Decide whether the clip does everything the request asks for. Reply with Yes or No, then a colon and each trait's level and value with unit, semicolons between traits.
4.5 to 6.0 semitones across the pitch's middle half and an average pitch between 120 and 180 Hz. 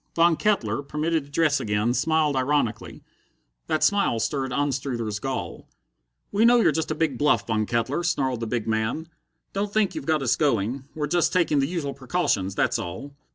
Yes: wide, 5.4 semitones; medium, 140 Hz